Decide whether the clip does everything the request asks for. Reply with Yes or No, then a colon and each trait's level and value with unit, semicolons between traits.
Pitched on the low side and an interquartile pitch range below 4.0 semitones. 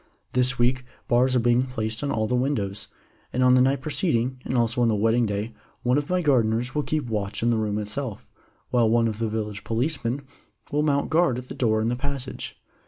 Yes: low, 120 Hz; average, 2.9 semitones